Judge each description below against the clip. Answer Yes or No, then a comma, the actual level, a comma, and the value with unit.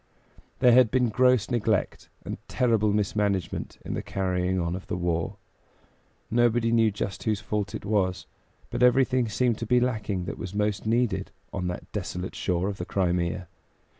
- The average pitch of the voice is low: Yes, low, 105 Hz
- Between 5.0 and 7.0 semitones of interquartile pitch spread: No, average, 4.3 semitones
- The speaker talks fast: No, average, 165 wpm